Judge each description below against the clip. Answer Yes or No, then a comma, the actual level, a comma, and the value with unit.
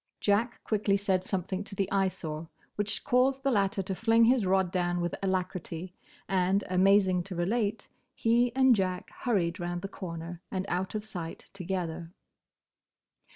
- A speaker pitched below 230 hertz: Yes, high, 190 Hz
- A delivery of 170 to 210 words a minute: No, average, 155 wpm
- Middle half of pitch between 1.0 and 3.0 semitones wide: Yes, average, 2.7 semitones